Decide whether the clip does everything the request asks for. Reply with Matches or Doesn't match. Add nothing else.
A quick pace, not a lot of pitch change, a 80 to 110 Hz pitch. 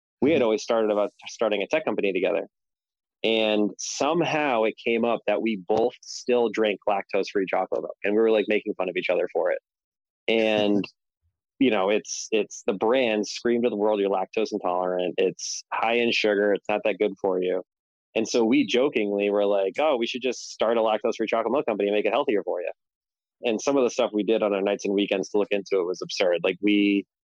Matches